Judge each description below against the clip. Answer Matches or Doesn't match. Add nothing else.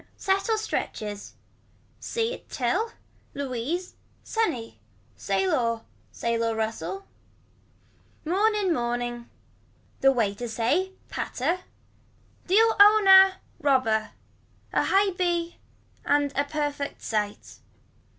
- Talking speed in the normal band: Doesn't match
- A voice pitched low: Doesn't match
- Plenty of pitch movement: Matches